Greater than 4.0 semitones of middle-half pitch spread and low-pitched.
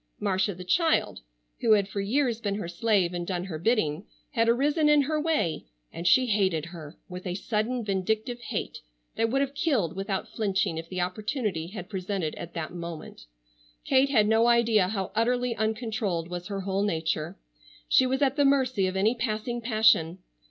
No: average, 4.9 semitones; high, 210 Hz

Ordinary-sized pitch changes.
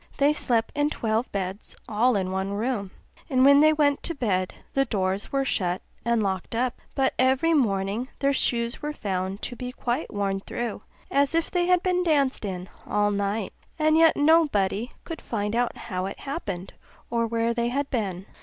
No: wide, 5.9 semitones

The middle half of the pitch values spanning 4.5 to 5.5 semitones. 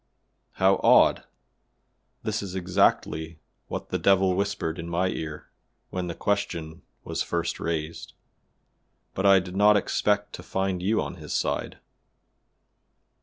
No: average, 2.9 semitones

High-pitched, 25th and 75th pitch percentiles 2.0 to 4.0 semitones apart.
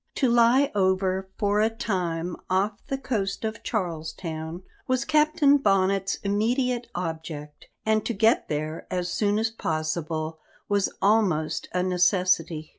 No: high, 195 Hz; average, 5.0 semitones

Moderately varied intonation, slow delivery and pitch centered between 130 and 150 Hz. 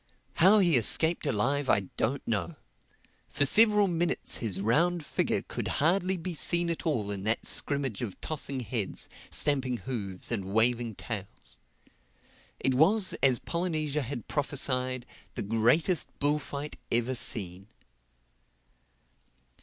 No: wide, 6.2 semitones; slow, 120 wpm; low, 135 Hz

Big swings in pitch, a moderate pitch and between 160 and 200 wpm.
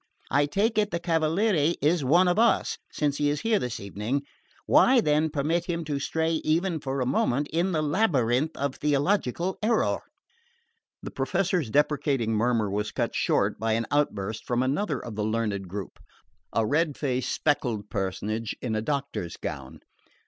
Yes: wide, 6.4 semitones; medium, 145 Hz; average, 165 wpm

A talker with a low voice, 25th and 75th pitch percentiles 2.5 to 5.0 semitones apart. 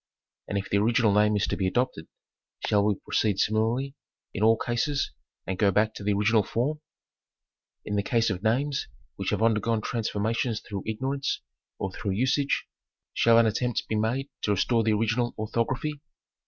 Yes: low, 110 Hz; average, 2.8 semitones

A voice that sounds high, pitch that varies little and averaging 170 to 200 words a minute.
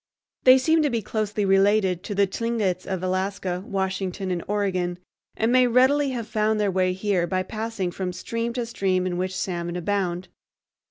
No: high, 195 Hz; average, 3.4 semitones; average, 175 wpm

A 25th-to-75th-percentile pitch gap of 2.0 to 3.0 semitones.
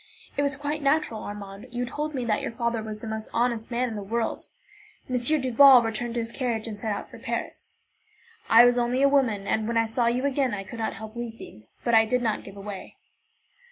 Yes: narrow, 2.5 semitones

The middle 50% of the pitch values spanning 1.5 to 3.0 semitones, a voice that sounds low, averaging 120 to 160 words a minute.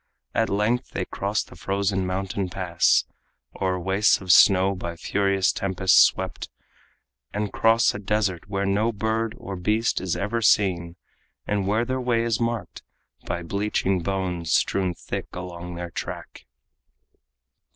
Yes: narrow, 2.6 semitones; very low, 95 Hz; average, 140 wpm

